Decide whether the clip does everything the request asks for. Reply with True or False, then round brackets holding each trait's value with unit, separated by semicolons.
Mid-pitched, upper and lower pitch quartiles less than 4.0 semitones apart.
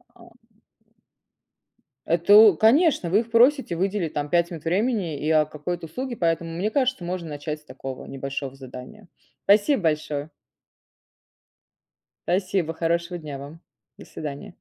False (170 Hz; 5.1 semitones)